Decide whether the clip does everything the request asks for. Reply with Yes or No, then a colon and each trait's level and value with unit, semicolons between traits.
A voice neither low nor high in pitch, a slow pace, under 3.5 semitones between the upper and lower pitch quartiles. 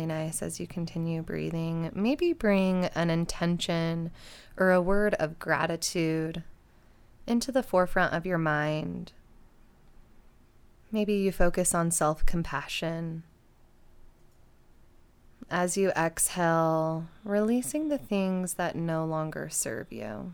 Yes: medium, 170 Hz; slow, 110 wpm; average, 2.7 semitones